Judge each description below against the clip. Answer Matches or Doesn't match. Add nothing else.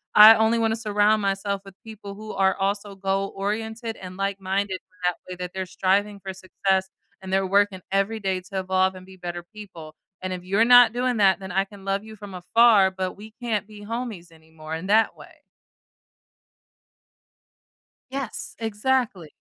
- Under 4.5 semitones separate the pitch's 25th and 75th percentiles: Matches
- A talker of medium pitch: Doesn't match